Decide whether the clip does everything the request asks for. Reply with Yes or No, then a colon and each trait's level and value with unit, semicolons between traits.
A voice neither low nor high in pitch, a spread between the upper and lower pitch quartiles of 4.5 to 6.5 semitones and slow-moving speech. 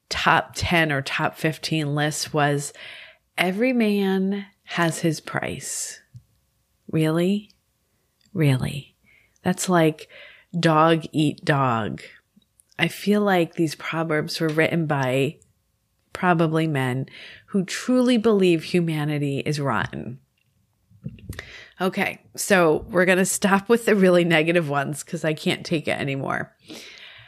No: medium, 165 Hz; average, 3.9 semitones; slow, 115 wpm